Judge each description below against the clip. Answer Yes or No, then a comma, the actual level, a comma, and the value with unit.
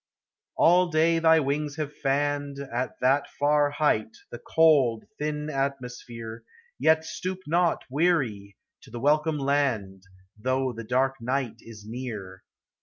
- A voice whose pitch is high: No, medium, 140 Hz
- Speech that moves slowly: Yes, slow, 130 wpm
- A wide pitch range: No, average, 4.1 semitones